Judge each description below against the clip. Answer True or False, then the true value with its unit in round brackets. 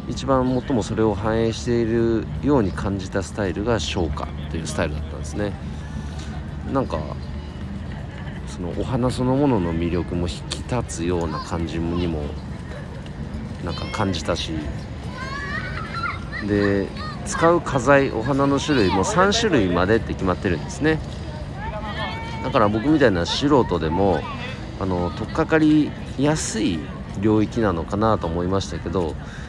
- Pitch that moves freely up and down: True (6.6 semitones)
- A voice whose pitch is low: True (95 Hz)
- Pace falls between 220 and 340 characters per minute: True (280 characters per minute)